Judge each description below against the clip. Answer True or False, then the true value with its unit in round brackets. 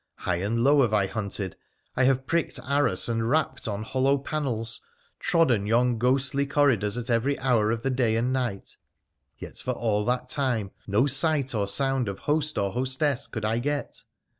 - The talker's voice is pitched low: True (125 Hz)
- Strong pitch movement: False (3.8 semitones)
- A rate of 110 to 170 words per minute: False (180 wpm)